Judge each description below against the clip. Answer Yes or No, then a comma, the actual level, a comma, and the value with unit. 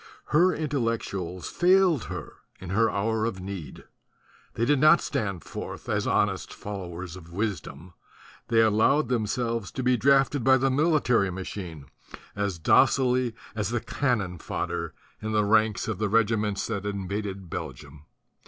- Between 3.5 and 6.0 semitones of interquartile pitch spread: Yes, average, 4.7 semitones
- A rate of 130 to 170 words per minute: Yes, average, 145 wpm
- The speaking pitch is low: Yes, low, 110 Hz